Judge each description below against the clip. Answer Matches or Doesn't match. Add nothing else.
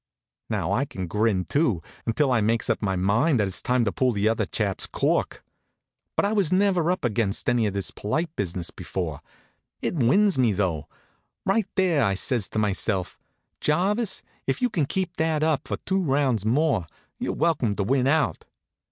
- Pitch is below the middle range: Matches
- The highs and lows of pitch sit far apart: Matches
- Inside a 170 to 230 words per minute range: Matches